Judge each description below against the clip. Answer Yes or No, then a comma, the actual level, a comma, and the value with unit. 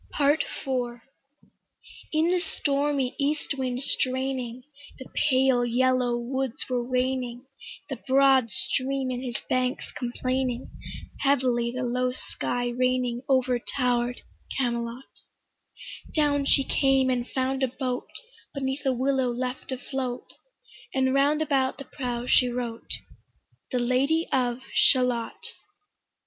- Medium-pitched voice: No, very high, 255 Hz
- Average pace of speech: No, slow, 120 wpm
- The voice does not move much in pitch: Yes, narrow, 1.6 semitones